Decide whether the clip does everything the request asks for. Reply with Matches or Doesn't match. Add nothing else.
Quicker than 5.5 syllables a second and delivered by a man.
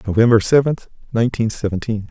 Matches